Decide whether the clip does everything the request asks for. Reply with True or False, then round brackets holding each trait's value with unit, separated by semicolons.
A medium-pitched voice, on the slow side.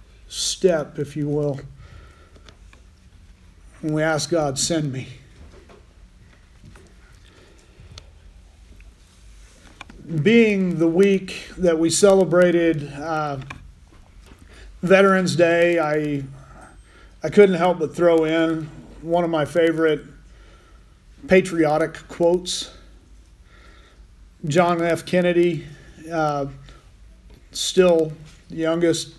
True (150 Hz; 80 wpm)